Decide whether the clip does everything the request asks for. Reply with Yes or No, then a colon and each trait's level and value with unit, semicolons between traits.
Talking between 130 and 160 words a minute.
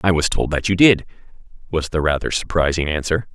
No: average, 195 wpm